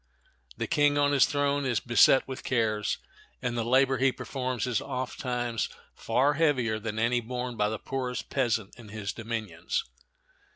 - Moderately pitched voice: No, low, 125 Hz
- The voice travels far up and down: No, average, 3.0 semitones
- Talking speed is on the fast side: No, average, 160 wpm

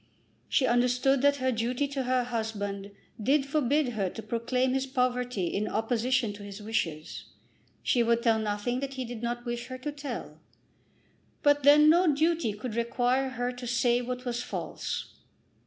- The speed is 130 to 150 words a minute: No, average, 170 wpm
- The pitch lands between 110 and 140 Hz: No, high, 245 Hz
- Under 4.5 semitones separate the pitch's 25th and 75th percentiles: Yes, average, 2.7 semitones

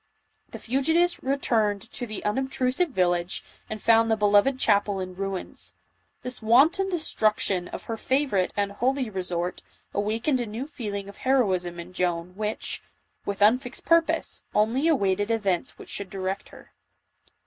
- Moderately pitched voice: No, high, 215 Hz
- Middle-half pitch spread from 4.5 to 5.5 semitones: Yes, average, 5.1 semitones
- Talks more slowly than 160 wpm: Yes, average, 145 wpm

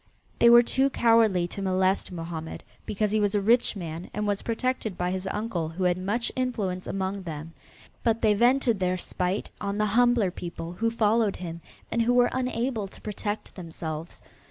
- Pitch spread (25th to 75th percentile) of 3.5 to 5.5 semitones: Yes, average, 4.2 semitones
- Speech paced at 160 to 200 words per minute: Yes, average, 180 wpm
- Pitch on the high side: Yes, high, 200 Hz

